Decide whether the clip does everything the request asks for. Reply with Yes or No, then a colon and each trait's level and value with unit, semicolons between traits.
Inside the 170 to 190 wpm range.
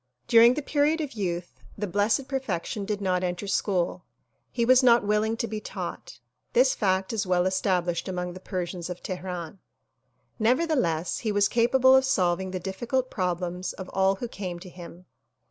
Yes: average, 175 wpm